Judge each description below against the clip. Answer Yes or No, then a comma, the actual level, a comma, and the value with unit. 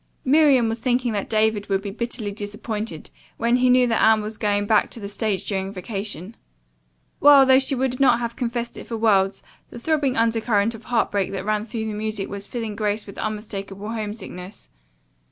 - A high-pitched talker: Yes, high, 220 Hz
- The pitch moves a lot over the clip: No, narrow, 2.6 semitones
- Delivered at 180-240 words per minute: Yes, average, 190 wpm